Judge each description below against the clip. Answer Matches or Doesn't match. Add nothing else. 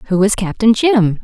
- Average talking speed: Matches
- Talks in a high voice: Matches